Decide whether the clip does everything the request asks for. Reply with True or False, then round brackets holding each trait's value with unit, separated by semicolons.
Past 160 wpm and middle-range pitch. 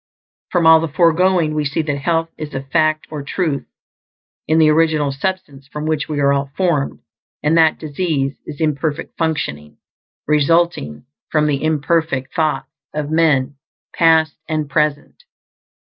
False (145 wpm; 155 Hz)